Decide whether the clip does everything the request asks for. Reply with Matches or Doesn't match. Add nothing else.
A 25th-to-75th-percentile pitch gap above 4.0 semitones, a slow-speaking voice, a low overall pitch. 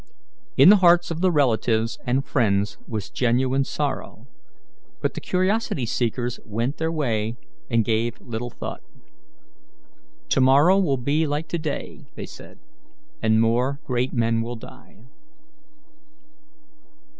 Matches